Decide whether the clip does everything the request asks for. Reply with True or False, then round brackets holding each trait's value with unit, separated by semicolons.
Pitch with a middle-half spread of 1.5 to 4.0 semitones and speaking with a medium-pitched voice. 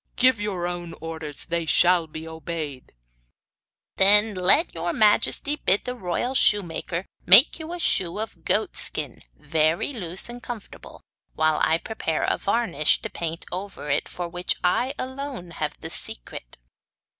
False (5.3 semitones; 180 Hz)